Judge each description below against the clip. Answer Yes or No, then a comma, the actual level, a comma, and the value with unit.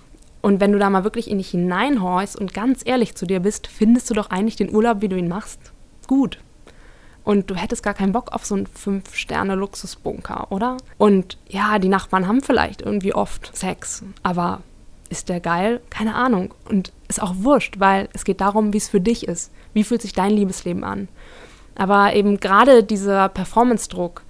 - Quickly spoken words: Yes, fast, 195 wpm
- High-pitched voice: Yes, high, 205 Hz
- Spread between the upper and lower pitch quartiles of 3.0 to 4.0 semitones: No, narrow, 2.6 semitones